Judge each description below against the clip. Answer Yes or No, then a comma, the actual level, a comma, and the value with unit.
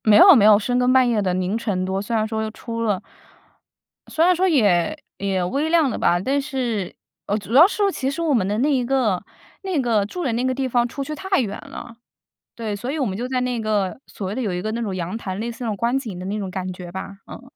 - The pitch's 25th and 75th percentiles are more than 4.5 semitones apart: Yes, average, 5.0 semitones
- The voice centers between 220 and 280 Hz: Yes, high, 230 Hz